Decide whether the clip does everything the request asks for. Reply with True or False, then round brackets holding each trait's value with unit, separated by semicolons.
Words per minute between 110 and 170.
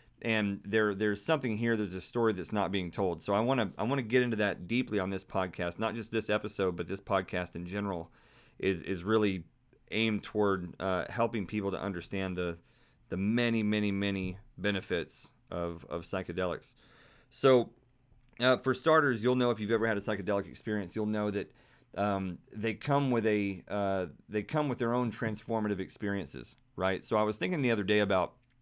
False (195 wpm)